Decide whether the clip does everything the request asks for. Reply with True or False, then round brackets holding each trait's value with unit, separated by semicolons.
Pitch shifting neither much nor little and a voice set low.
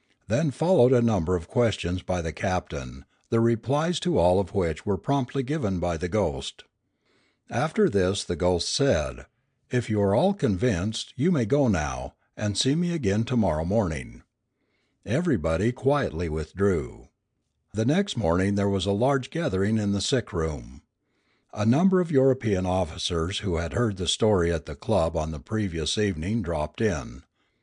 False (5.9 semitones; 100 Hz)